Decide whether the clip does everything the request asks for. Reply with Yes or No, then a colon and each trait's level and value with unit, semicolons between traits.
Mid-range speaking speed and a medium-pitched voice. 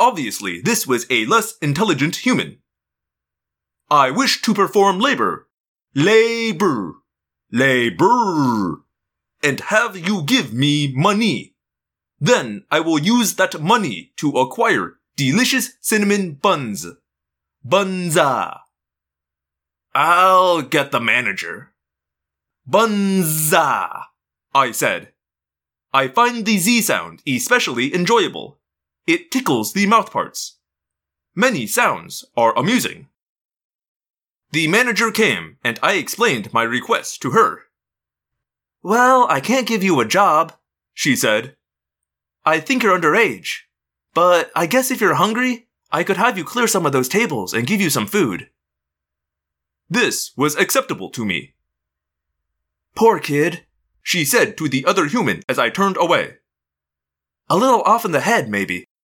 No: slow, 125 wpm; medium, 150 Hz